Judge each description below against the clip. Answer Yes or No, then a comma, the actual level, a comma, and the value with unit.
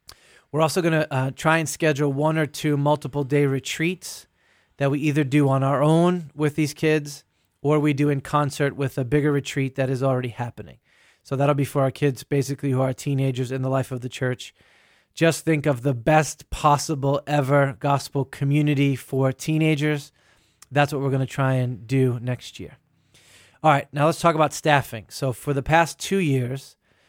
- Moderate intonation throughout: No, narrow, 2.1 semitones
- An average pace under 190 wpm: No, average, 195 wpm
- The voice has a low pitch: No, medium, 145 Hz